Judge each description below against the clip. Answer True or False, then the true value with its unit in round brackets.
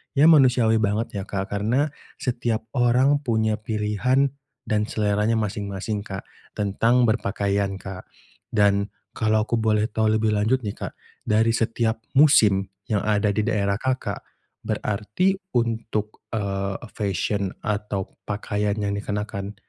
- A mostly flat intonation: True (2.2 semitones)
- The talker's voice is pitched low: True (105 Hz)